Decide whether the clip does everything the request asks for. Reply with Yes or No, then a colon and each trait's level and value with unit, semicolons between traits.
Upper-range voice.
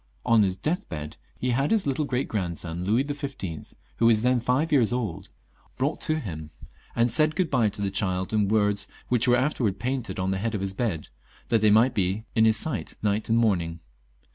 No: low, 110 Hz